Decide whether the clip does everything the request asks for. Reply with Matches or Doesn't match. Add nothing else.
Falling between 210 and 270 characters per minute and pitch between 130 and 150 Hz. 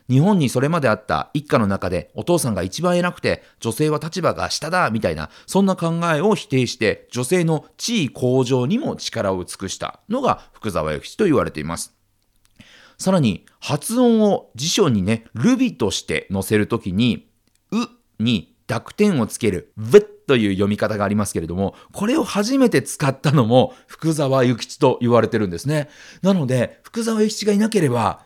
Doesn't match